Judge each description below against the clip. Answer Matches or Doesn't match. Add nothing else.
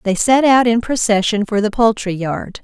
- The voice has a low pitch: Doesn't match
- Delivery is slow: Doesn't match